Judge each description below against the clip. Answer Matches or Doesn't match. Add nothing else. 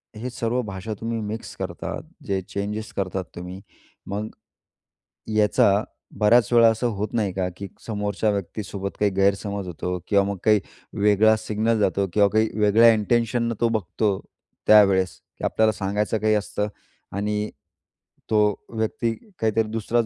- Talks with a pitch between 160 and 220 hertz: Doesn't match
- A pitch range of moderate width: Doesn't match